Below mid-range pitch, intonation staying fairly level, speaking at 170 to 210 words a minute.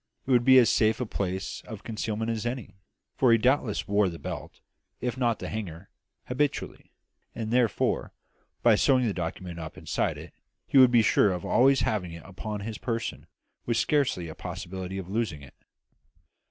No: low, 110 Hz; average, 4.5 semitones; average, 180 wpm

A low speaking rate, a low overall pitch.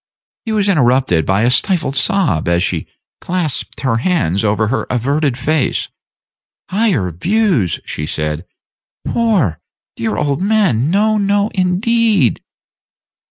No: slow, 120 wpm; medium, 145 Hz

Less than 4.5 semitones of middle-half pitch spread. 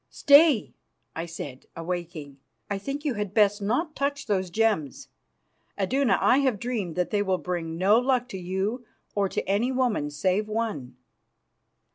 No: wide, 5.6 semitones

